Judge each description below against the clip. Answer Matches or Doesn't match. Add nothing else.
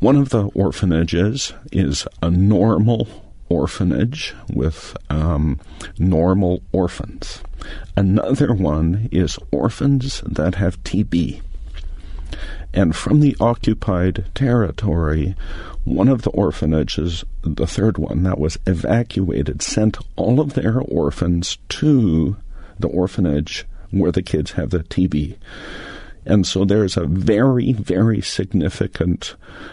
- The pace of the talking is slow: Matches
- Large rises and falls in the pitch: Doesn't match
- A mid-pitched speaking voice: Doesn't match